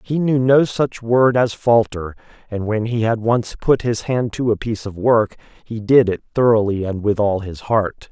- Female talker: No, male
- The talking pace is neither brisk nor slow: No, fast, 215 wpm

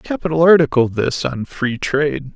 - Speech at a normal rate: Yes, average, 155 wpm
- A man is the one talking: Yes, male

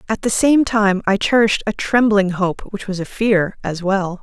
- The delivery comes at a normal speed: No, fast, 215 wpm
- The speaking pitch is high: Yes, high, 205 Hz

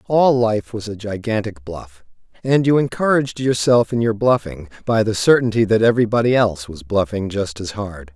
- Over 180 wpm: No, average, 175 wpm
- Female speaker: No, male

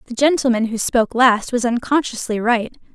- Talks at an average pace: Yes, average, 165 wpm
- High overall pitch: Yes, high, 240 Hz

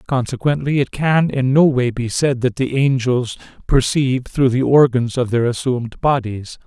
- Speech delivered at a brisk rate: No, average, 170 wpm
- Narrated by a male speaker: Yes, male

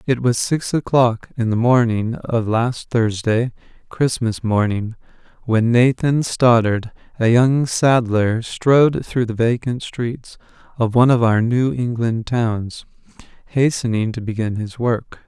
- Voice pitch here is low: Yes, low, 120 Hz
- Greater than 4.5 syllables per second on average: No, 3.8 syllables/s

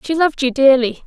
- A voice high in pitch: Yes, very high, 270 Hz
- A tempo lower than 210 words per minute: No, fast, 225 wpm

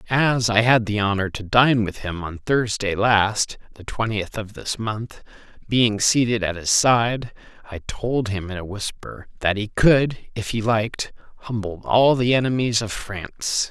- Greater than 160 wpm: Yes, average, 175 wpm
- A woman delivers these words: No, male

